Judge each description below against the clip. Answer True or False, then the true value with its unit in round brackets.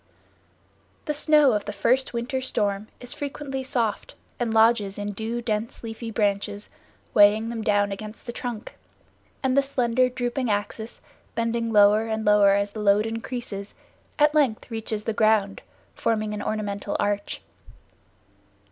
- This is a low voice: False (220 Hz)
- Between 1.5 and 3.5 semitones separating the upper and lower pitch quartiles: True (2.8 semitones)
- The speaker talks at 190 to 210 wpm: False (145 wpm)